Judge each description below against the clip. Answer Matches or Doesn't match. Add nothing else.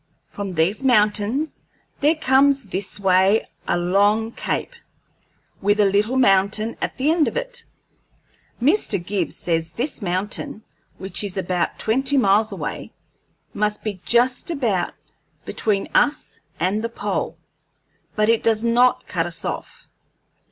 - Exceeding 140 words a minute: Doesn't match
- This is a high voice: Matches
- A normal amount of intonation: Matches